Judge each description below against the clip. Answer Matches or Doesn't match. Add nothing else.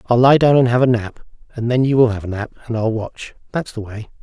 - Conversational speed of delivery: Doesn't match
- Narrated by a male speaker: Matches